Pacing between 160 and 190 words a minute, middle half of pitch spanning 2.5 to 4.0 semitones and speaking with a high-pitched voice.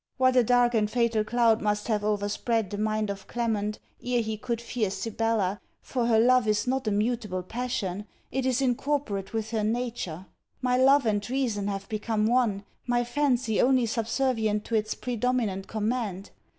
Yes: average, 170 wpm; average, 2.9 semitones; high, 225 Hz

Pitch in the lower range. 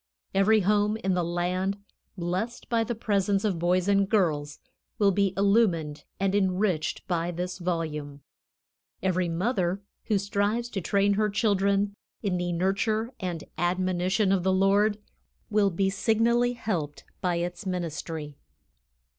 No: high, 190 Hz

